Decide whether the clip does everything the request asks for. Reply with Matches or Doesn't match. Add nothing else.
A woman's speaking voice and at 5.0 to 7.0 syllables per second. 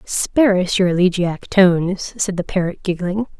Doesn't match